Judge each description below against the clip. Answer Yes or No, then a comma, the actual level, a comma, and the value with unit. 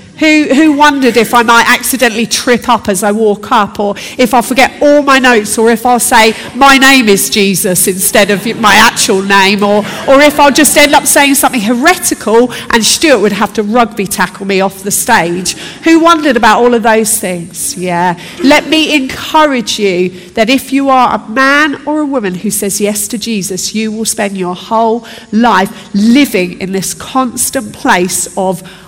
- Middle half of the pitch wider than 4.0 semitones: Yes, average, 4.9 semitones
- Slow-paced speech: No, average, 195 wpm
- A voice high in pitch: Yes, high, 225 Hz